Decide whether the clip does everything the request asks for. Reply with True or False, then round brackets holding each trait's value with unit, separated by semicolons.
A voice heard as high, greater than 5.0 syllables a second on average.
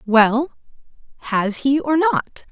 False (265 Hz; 3.1 syllables/s)